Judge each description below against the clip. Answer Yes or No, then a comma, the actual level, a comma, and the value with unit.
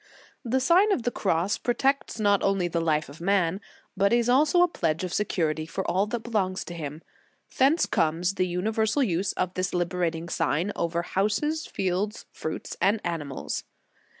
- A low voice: No, high, 190 Hz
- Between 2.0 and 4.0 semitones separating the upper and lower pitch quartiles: No, average, 4.8 semitones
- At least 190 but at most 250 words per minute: No, average, 175 wpm